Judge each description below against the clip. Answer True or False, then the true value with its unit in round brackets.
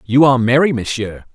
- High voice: False (125 Hz)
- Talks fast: False (180 wpm)